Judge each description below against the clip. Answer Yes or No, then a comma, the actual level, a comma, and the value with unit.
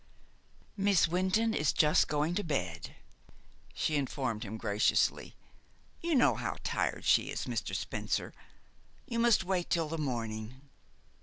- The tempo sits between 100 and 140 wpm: Yes, slow, 135 wpm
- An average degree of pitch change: No, wide, 8.2 semitones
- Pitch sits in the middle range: Yes, medium, 155 Hz